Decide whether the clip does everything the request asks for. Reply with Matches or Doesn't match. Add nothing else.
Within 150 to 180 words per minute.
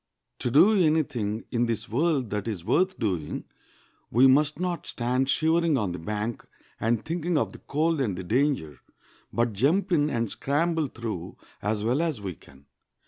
Matches